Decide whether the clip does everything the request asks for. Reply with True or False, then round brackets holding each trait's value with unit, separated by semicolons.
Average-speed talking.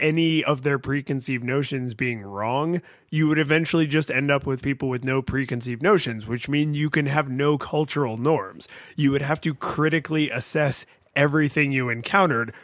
True (170 wpm)